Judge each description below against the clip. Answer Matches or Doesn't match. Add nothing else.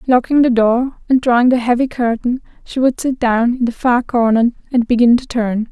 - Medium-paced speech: Doesn't match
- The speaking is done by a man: Doesn't match